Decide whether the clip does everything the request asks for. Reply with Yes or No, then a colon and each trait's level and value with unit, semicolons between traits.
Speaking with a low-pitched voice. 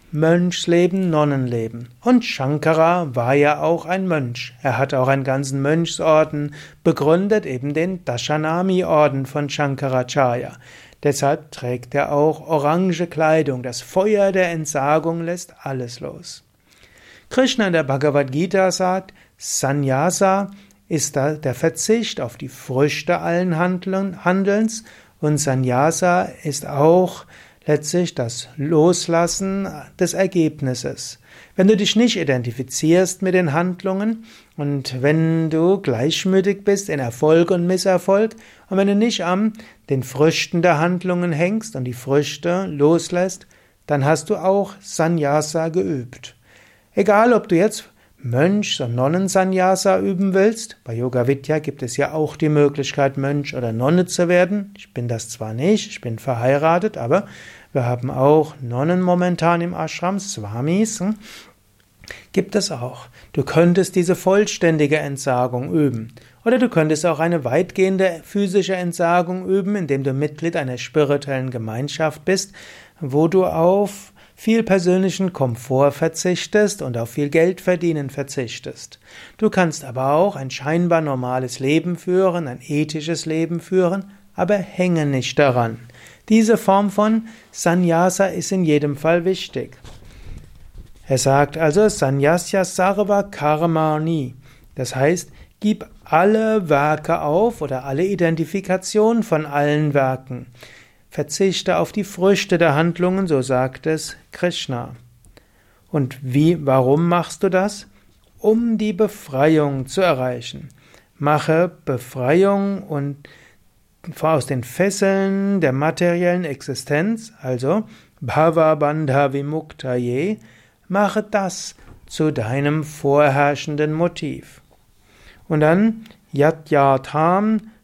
No: medium, 160 Hz